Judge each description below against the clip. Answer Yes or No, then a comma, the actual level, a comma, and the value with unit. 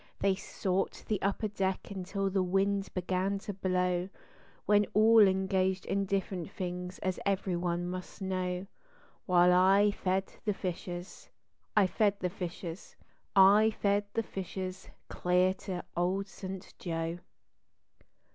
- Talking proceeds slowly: Yes, slow, 130 wpm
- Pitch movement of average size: No, narrow, 1.6 semitones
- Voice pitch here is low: No, high, 190 Hz